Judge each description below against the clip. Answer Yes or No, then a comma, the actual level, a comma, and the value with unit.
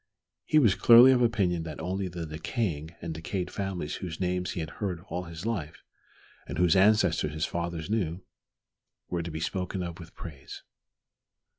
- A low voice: Yes, very low, 90 Hz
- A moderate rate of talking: Yes, average, 170 wpm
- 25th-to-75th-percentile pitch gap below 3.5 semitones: Yes, average, 3.0 semitones